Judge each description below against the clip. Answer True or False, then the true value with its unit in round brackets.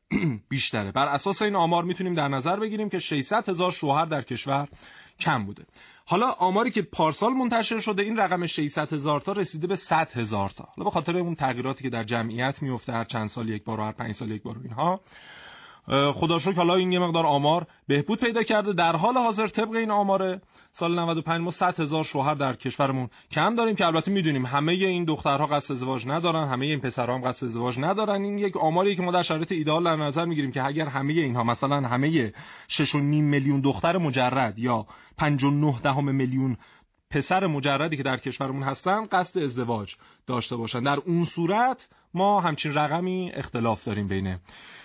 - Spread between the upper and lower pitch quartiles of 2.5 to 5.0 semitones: False (5.4 semitones)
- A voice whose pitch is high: False (155 Hz)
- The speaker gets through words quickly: True (185 wpm)